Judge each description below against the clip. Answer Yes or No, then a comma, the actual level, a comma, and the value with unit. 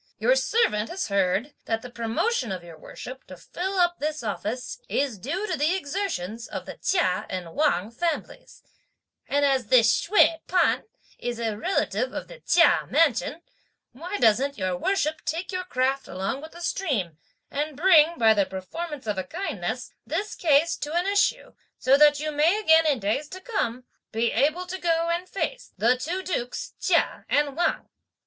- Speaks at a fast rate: No, average, 175 wpm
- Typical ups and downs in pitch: No, wide, 7.3 semitones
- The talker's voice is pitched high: Yes, very high, 295 Hz